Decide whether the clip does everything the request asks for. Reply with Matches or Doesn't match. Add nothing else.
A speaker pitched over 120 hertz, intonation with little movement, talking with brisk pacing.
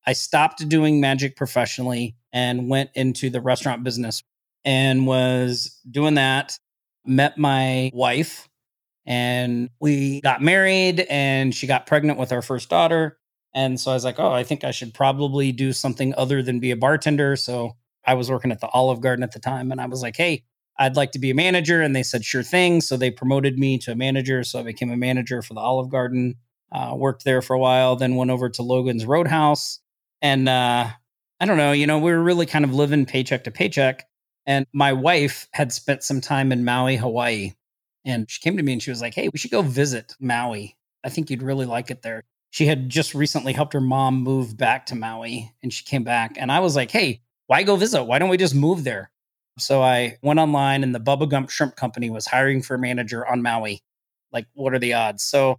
Matches